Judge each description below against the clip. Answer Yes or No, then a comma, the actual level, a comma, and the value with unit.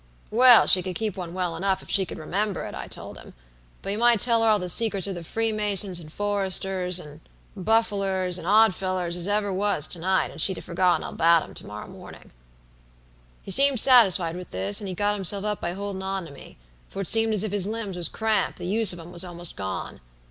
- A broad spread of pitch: No, average, 2.9 semitones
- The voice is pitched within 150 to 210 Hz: Yes, high, 190 Hz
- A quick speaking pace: Yes, fast, 230 wpm